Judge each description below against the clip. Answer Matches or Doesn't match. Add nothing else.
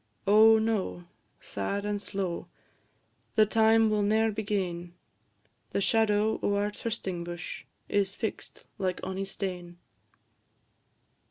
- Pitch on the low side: Doesn't match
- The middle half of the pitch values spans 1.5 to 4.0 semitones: Matches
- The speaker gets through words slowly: Matches